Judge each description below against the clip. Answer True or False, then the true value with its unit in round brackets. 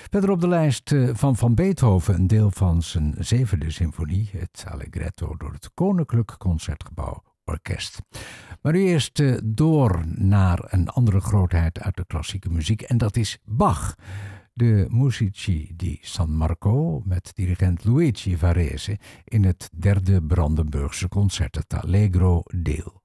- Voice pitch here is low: True (95 Hz)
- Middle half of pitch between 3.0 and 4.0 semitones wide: False (4.8 semitones)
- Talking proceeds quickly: False (140 wpm)